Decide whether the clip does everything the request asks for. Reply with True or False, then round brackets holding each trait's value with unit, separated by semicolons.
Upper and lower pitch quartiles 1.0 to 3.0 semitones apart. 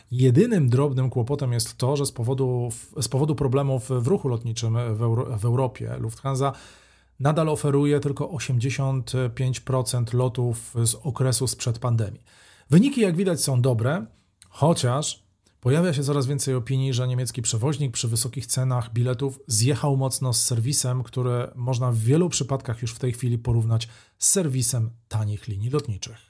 True (2.6 semitones)